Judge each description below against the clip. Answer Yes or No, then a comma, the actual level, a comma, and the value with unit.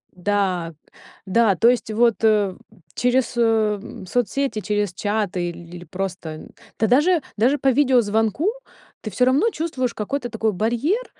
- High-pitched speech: Yes, high, 225 Hz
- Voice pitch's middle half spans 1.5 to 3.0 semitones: No, average, 4.2 semitones